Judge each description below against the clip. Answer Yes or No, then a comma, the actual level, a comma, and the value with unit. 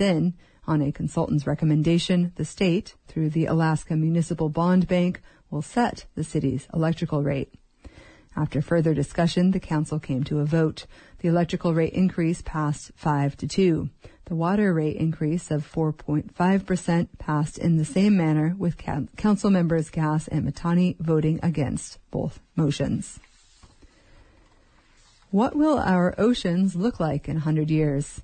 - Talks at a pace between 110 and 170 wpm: Yes, average, 140 wpm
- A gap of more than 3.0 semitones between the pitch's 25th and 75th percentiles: No, average, 2.7 semitones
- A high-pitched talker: No, medium, 165 Hz